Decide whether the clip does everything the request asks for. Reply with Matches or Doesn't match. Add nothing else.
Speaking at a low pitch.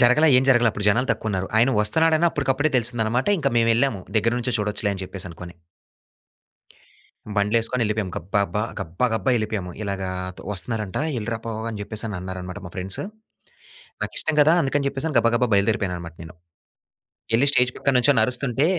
Matches